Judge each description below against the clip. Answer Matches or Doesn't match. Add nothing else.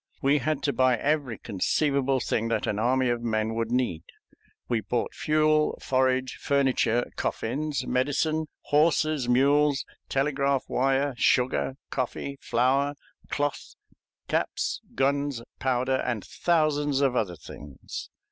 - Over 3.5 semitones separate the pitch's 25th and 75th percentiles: Doesn't match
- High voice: Doesn't match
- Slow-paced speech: Matches